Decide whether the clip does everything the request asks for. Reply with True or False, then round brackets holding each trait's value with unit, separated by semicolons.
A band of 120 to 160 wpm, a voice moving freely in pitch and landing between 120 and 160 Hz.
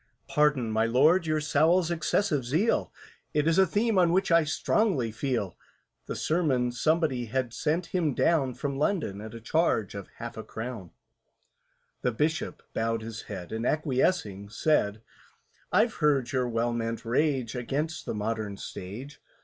True (155 wpm; 5.9 semitones; 135 Hz)